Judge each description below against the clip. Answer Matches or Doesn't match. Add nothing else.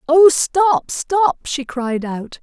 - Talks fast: Doesn't match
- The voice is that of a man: Doesn't match